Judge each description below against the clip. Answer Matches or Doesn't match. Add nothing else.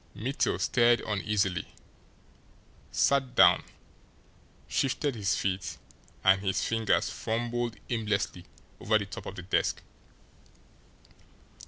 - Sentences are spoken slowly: Matches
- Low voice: Matches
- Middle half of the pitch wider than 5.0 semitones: Doesn't match